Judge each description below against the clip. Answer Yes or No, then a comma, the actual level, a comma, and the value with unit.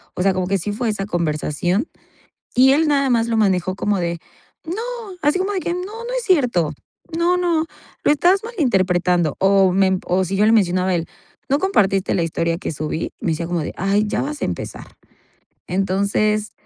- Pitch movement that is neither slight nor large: No, wide, 8.3 semitones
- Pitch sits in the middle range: No, high, 200 Hz